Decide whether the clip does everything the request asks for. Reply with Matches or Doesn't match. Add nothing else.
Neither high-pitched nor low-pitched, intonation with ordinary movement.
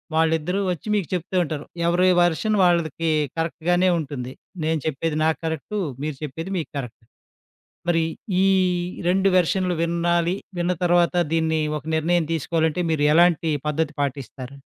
Doesn't match